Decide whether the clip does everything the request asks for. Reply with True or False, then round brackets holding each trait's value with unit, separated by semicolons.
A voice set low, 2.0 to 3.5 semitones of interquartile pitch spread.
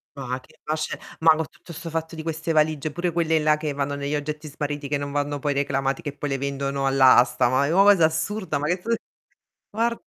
False (150 Hz; 2.4 semitones)